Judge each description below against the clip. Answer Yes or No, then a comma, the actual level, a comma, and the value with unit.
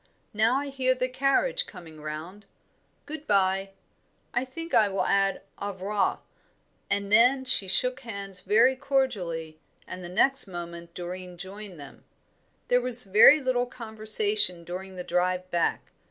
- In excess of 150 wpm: No, average, 145 wpm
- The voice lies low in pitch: No, high, 200 Hz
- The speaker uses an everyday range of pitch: No, wide, 5.9 semitones